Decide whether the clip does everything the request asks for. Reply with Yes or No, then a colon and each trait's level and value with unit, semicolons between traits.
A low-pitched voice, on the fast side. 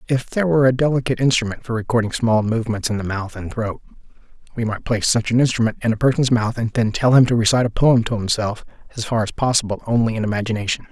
Yes: low, 115 Hz; fast, 230 wpm